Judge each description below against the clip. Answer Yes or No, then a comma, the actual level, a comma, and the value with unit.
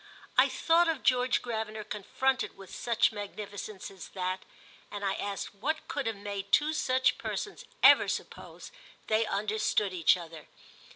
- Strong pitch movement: No, average, 4.3 semitones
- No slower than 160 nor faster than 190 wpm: No, average, 150 wpm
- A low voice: No, high, 215 Hz